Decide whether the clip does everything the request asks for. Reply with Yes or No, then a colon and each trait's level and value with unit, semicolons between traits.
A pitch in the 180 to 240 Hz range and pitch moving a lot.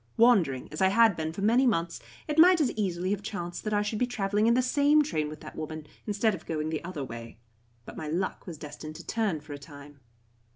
Yes: high, 190 Hz; wide, 6.3 semitones